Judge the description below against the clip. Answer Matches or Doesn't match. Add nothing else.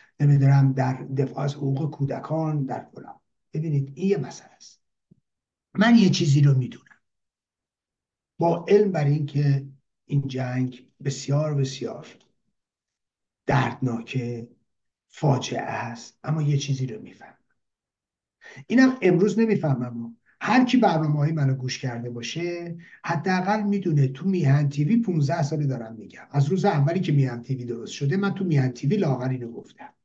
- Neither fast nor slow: Matches